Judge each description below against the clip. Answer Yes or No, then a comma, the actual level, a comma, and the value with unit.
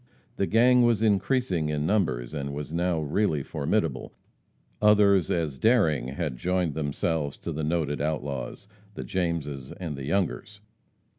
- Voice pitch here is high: No, very low, 80 Hz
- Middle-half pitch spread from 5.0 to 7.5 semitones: Yes, wide, 5.5 semitones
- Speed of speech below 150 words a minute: Yes, average, 140 wpm